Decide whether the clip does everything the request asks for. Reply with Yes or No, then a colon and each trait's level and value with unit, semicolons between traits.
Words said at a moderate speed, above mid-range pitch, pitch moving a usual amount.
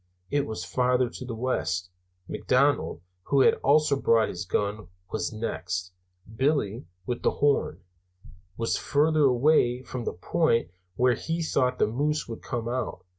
No: average, 150 wpm; low, 125 Hz; average, 4.4 semitones